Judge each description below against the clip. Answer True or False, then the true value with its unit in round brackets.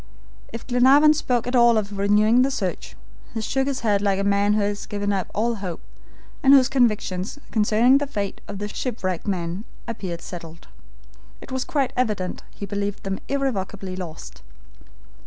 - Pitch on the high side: True (210 Hz)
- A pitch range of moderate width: True (4.2 semitones)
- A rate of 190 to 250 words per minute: False (170 wpm)